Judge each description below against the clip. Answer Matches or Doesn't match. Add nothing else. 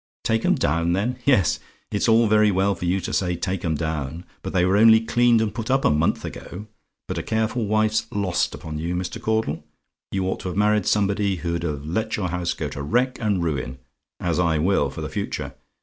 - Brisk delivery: Matches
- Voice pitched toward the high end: Doesn't match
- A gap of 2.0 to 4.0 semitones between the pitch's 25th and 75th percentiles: Doesn't match